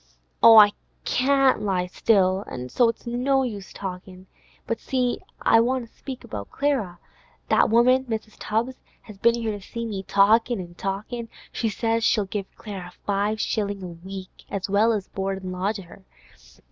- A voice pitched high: Yes, high, 210 Hz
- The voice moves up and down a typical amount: Yes, average, 3.4 semitones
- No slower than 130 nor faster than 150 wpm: No, average, 170 wpm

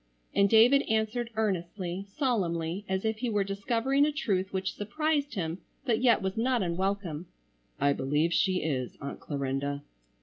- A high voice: Yes, high, 195 Hz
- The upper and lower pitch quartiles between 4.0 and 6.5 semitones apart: Yes, average, 5.1 semitones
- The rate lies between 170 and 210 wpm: No, average, 155 wpm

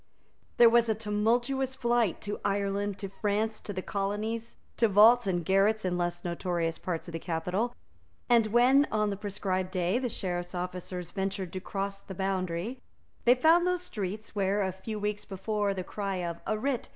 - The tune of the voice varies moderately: Yes, average, 3.3 semitones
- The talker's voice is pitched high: Yes, high, 200 Hz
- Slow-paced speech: No, average, 180 wpm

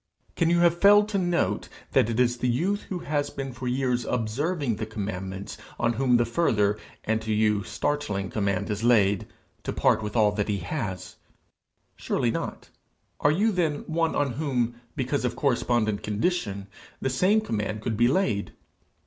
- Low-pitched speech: Yes, low, 120 Hz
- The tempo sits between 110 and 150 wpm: No, average, 175 wpm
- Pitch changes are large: Yes, wide, 5.8 semitones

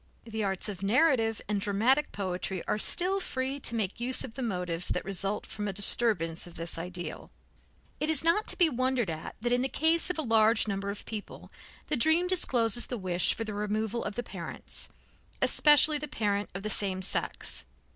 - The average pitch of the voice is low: No, high, 220 Hz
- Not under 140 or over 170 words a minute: No, average, 195 wpm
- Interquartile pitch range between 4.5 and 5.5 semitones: Yes, average, 4.9 semitones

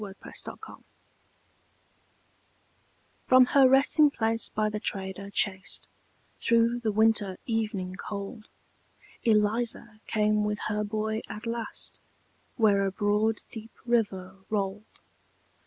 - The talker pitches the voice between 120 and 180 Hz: No, high, 215 Hz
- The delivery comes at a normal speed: No, slow, 115 wpm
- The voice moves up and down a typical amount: No, narrow, 2.0 semitones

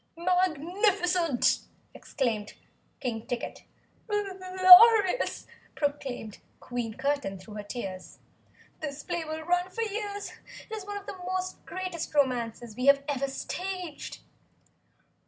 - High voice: Yes, very high, 330 Hz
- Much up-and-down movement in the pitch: Yes, wide, 6.8 semitones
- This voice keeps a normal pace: No, slow, 110 wpm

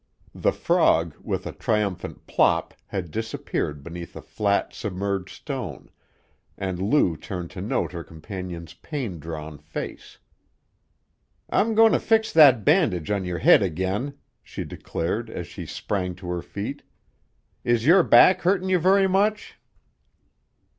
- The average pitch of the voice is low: Yes, low, 100 Hz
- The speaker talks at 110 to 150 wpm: Yes, average, 140 wpm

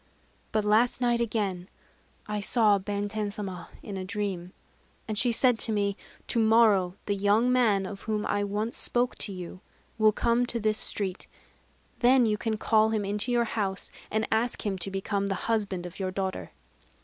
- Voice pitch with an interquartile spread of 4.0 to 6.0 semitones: No, narrow, 2.4 semitones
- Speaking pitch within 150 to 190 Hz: No, high, 210 Hz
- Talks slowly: No, average, 180 wpm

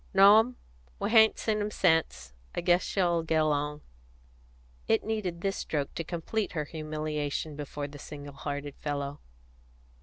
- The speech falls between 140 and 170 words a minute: Yes, average, 150 wpm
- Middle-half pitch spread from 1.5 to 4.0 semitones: No, average, 5.0 semitones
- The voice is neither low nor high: Yes, medium, 160 Hz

